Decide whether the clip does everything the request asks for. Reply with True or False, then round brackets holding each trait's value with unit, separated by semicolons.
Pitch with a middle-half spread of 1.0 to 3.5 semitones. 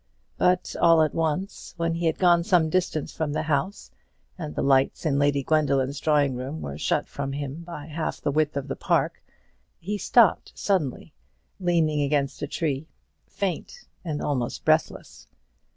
True (3.2 semitones)